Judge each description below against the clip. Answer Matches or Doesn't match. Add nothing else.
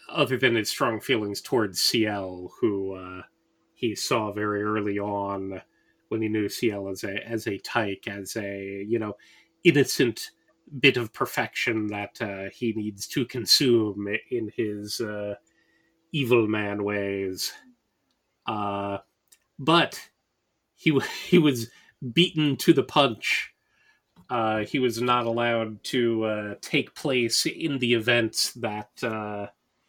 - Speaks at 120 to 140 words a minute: Matches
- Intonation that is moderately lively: Matches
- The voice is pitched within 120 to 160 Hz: Doesn't match